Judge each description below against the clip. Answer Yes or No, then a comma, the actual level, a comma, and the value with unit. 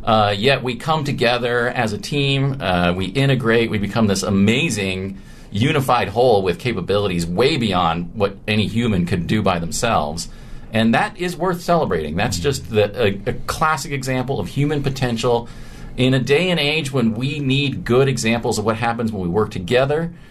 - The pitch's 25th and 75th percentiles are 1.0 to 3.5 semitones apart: No, average, 5.0 semitones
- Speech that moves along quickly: No, average, 175 wpm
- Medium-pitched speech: No, low, 120 Hz